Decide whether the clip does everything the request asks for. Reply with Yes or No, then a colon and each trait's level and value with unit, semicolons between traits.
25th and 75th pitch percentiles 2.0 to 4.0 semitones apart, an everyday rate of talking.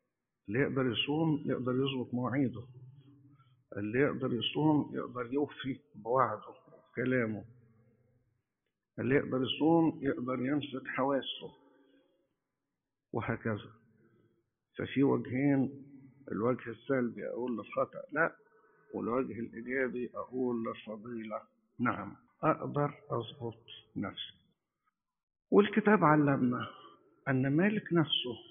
No: average, 3.0 semitones; slow, 85 wpm